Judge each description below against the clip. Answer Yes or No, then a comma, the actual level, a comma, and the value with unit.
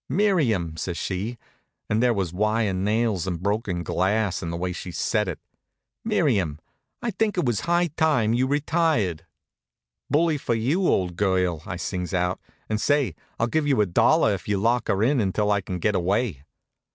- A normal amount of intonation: No, wide, 6.6 semitones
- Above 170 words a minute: Yes, average, 180 wpm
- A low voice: Yes, low, 105 Hz